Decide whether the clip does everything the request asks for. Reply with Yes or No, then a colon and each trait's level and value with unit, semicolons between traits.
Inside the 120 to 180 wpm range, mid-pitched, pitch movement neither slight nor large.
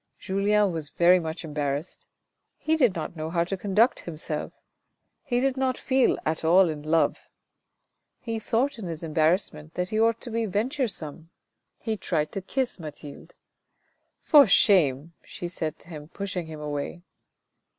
No: average, 160 wpm; medium, 180 Hz; wide, 5.9 semitones